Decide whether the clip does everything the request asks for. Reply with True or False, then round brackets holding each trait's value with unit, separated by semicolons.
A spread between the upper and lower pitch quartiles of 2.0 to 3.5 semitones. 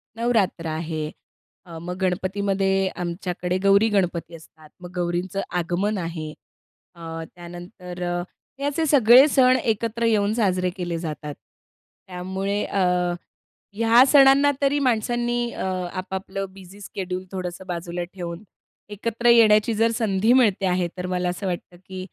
False (4.0 semitones)